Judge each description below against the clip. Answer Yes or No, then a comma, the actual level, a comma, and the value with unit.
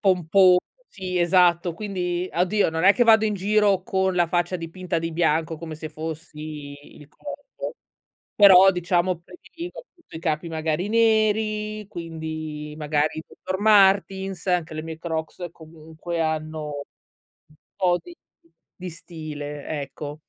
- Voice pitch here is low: No, medium, 175 Hz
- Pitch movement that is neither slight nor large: Yes, average, 3.5 semitones